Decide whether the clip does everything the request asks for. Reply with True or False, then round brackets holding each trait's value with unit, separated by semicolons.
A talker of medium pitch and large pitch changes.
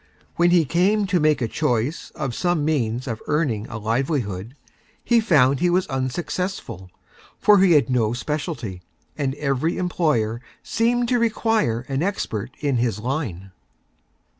True (145 Hz; 6.9 semitones)